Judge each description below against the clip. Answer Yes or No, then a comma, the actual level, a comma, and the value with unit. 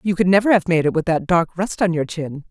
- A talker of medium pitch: Yes, medium, 175 Hz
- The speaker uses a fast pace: Yes, fast, 310 wpm